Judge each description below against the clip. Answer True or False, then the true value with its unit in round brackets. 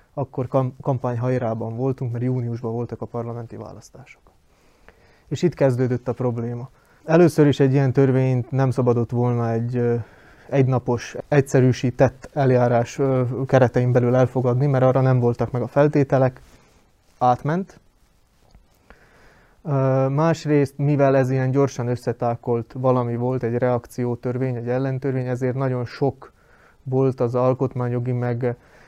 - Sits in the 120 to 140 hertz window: True (125 Hz)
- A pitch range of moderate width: False (1.8 semitones)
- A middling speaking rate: True (115 wpm)